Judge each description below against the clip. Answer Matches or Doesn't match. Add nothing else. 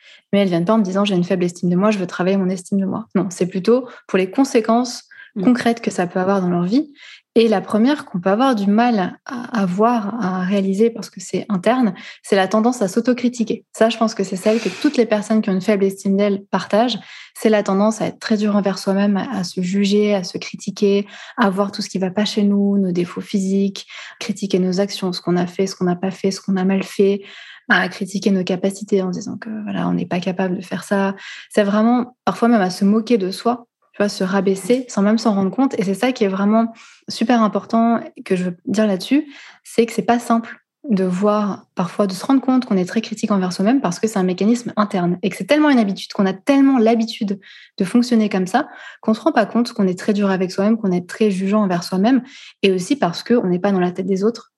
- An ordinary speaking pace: Doesn't match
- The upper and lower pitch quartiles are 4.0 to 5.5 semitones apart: Doesn't match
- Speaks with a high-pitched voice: Matches